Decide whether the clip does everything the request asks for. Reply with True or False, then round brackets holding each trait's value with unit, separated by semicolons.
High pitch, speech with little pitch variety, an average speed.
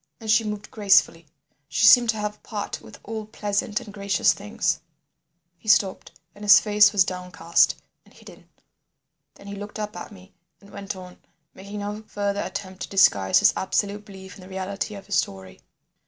True (200 Hz; 1.6 semitones; 180 wpm)